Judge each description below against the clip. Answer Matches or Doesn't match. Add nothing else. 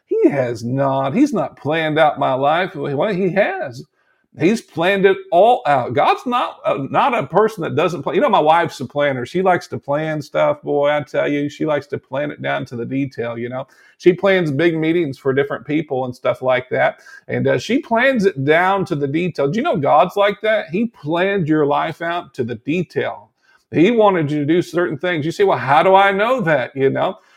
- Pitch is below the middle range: Doesn't match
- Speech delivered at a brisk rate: Matches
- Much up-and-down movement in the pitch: Matches